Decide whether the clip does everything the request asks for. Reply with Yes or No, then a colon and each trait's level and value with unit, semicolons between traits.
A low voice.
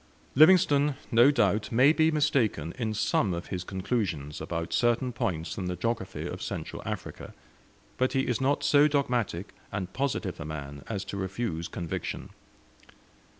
Yes: low, 110 Hz